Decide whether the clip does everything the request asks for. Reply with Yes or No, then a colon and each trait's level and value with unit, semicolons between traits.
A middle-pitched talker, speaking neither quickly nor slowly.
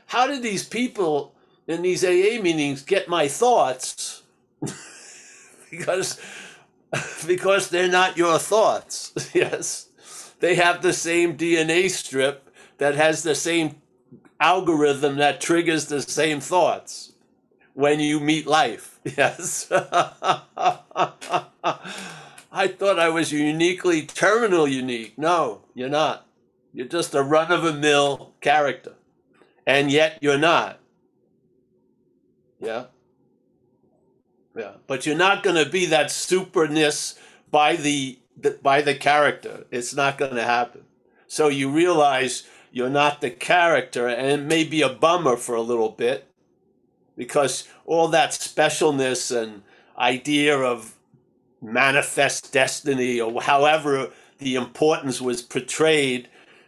No: medium, 150 Hz; slow, 120 wpm